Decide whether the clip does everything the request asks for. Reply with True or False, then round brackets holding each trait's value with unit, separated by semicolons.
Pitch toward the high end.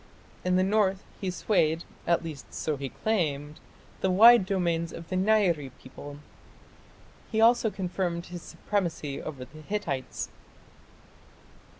False (175 Hz)